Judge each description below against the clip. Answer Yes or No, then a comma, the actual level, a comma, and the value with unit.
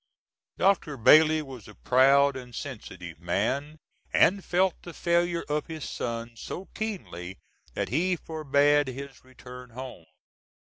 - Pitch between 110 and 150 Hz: Yes, medium, 140 Hz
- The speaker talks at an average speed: No, slow, 130 wpm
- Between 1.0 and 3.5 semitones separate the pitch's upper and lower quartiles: No, average, 4.6 semitones